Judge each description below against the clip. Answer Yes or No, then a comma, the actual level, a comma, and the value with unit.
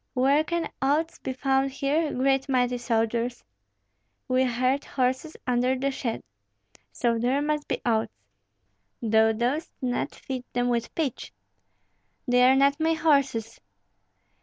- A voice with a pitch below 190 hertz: No, very high, 260 Hz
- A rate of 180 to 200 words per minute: No, slow, 135 wpm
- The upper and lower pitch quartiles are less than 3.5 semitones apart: Yes, narrow, 2.4 semitones